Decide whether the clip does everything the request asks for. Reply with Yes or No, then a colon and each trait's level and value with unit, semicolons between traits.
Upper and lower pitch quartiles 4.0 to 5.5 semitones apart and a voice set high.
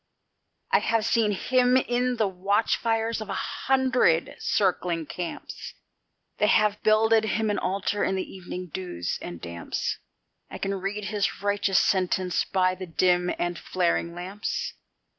No: average, 3.4 semitones; high, 195 Hz